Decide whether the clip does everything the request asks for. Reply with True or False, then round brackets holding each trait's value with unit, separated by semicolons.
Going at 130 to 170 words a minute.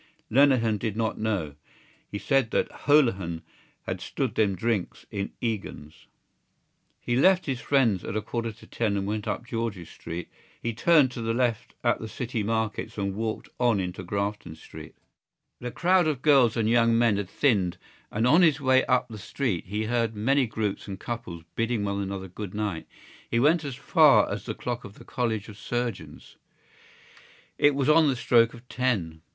False (180 wpm)